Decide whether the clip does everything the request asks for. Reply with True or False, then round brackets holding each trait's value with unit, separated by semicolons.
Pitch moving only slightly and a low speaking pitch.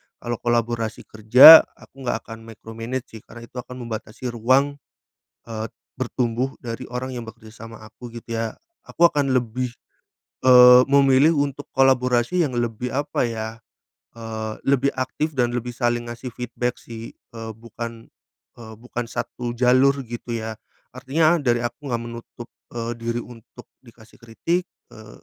True (2.1 semitones; 120 Hz)